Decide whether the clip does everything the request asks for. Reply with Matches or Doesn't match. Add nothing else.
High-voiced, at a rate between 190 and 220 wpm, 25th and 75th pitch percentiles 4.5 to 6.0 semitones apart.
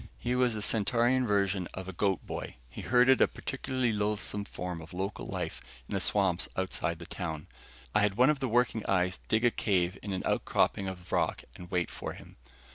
Doesn't match